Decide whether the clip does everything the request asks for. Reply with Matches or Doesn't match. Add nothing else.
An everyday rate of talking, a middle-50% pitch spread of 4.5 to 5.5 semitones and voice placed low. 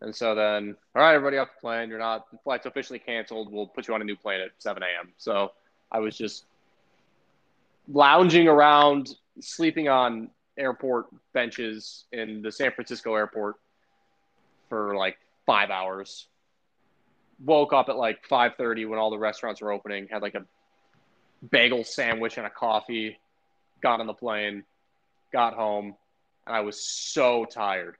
Doesn't match